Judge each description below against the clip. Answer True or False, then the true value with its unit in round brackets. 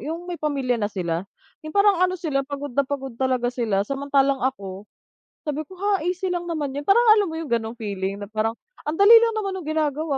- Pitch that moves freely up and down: True (6.4 semitones)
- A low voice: False (280 Hz)